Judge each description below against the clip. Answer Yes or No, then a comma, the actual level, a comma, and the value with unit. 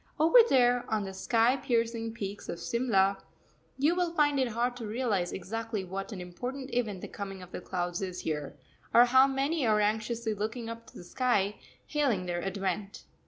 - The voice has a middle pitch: No, high, 225 Hz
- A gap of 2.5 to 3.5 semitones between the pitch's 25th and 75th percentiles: No, average, 4.3 semitones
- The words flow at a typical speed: Yes, average, 185 wpm